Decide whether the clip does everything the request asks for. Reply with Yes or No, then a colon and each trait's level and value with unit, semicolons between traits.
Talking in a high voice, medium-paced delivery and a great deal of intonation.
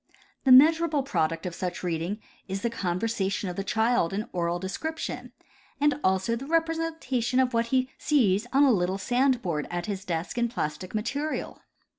Yes: high, 225 Hz; average, 180 wpm; wide, 6.2 semitones